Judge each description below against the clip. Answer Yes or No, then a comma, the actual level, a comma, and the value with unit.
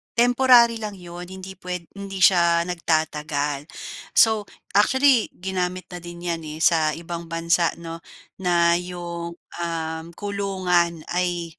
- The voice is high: No, medium, 175 Hz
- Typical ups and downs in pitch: No, narrow, 2.2 semitones